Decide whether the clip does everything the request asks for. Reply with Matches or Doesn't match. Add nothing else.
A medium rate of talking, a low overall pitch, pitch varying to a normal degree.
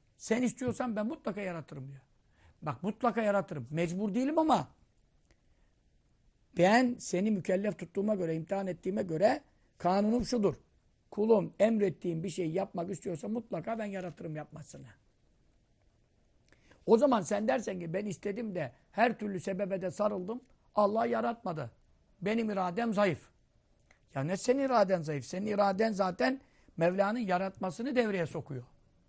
Doesn't match